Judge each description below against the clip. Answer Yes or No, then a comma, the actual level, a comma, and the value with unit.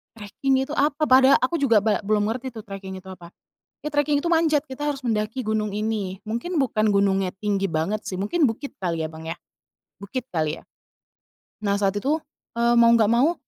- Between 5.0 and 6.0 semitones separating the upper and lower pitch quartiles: Yes, average, 5.3 semitones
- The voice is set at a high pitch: Yes, high, 215 Hz